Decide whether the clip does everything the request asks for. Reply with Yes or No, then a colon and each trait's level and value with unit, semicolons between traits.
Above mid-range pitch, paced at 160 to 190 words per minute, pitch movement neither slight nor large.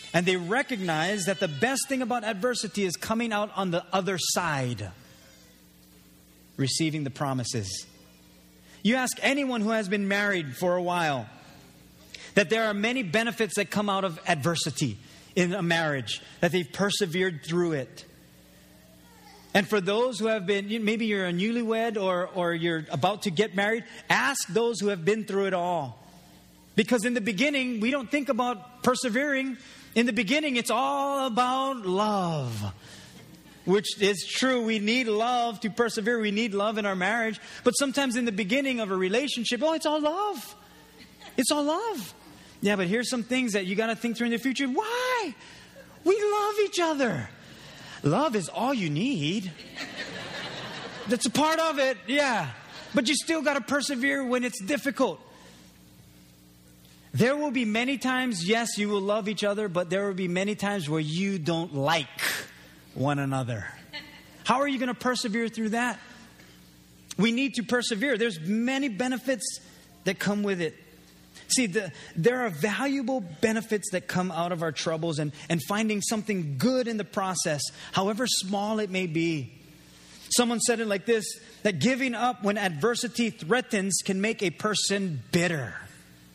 No: high, 205 Hz; average, 165 wpm; wide, 6.7 semitones